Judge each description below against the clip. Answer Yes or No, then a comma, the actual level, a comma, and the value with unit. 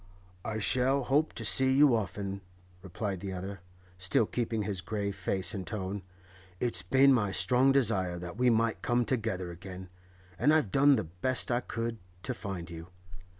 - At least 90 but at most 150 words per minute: No, average, 170 wpm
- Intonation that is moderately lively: Yes, average, 4.9 semitones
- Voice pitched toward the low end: Yes, low, 105 Hz